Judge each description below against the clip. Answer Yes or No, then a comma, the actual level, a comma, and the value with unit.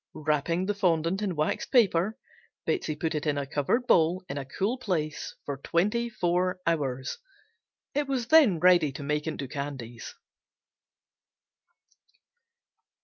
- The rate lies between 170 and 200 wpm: No, slow, 135 wpm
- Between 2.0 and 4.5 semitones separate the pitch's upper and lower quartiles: No, wide, 5.5 semitones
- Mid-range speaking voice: Yes, medium, 165 Hz